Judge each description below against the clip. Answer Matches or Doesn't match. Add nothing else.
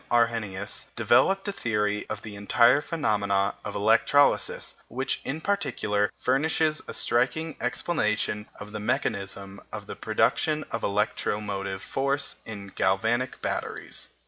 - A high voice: Doesn't match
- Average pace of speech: Doesn't match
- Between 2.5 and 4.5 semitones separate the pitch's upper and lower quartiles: Doesn't match